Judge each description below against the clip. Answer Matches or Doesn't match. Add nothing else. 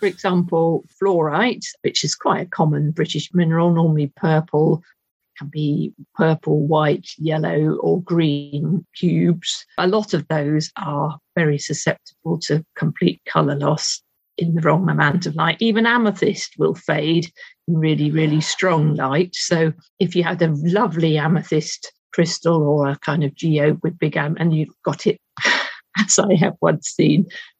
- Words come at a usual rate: Matches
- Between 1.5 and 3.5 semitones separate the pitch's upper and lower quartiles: Matches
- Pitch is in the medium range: Matches